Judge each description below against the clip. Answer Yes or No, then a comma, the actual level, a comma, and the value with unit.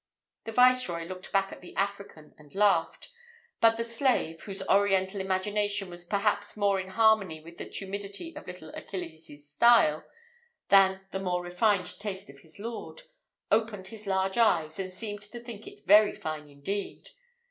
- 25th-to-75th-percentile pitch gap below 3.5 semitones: Yes, average, 2.8 semitones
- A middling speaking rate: Yes, average, 160 wpm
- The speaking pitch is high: Yes, high, 195 Hz